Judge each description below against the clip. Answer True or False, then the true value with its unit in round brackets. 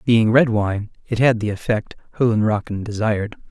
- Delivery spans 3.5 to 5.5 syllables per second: True (5.2 syllables/s)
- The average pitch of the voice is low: True (110 Hz)